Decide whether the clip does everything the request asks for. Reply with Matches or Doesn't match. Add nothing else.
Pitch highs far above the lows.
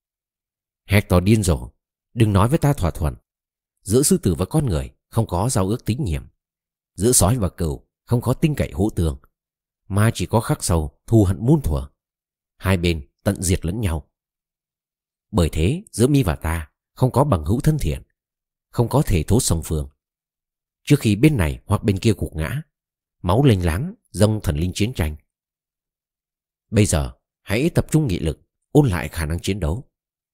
Matches